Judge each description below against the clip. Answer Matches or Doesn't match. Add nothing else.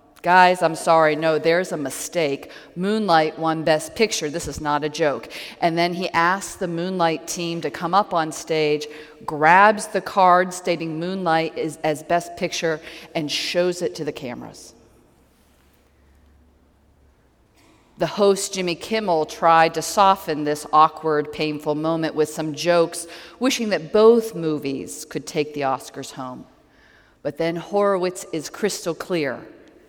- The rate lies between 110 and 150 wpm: Matches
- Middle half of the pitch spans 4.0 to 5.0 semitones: Doesn't match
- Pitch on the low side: Doesn't match